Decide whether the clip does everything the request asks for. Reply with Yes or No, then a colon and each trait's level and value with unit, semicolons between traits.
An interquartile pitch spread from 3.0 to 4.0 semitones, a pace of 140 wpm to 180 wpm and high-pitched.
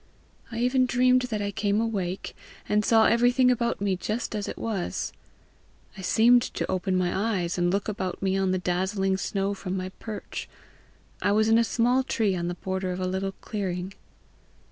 No: average, 3.4 semitones; average, 190 wpm; high, 200 Hz